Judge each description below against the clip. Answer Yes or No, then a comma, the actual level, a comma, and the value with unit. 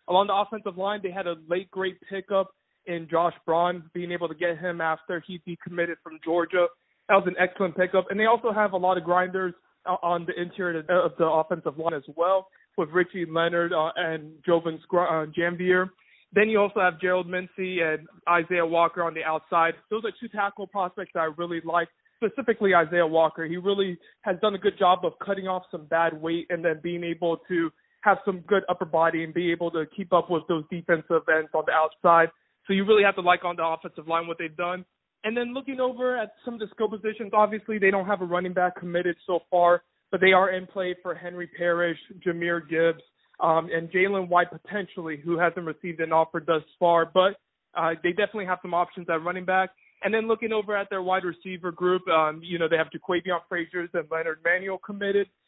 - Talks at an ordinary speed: No, fast, 215 wpm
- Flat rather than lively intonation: Yes, narrow, 2.3 semitones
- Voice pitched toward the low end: No, medium, 175 Hz